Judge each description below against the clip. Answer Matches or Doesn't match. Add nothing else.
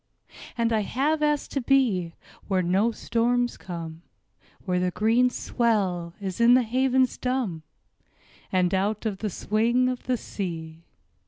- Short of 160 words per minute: Matches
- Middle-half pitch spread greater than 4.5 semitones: Matches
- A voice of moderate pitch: Doesn't match